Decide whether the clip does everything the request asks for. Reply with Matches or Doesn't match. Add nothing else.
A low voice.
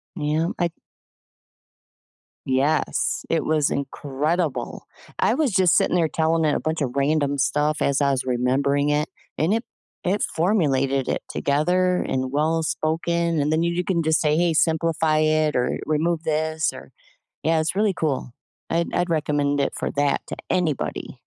Doesn't match